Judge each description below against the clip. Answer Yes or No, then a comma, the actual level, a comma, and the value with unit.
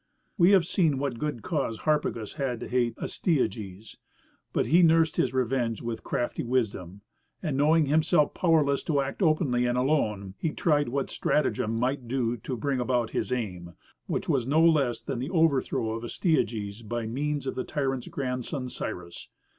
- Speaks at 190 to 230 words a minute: No, average, 170 wpm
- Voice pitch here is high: No, low, 130 Hz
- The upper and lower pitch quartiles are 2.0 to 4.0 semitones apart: No, average, 4.4 semitones